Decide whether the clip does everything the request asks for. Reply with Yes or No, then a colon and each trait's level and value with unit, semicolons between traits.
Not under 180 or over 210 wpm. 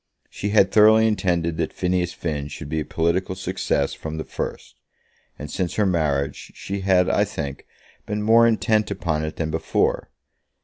No: average, 170 wpm